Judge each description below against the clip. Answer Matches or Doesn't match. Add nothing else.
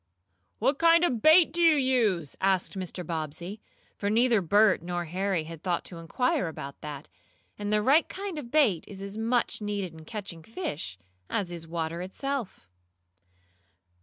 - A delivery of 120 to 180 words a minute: Matches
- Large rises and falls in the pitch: Matches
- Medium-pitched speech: Doesn't match